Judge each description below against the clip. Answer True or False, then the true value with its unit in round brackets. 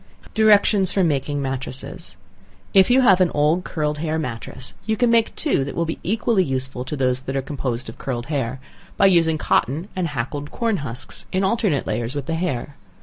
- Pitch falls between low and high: True (150 Hz)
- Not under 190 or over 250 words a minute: True (195 wpm)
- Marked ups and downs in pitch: True (6.2 semitones)